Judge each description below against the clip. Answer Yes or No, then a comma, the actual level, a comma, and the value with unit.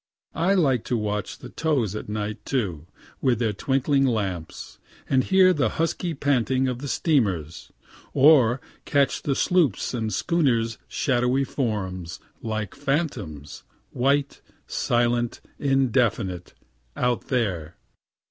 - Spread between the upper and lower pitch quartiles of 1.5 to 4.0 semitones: No, average, 4.6 semitones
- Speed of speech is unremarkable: No, slow, 120 wpm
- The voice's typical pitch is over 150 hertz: No, low, 125 Hz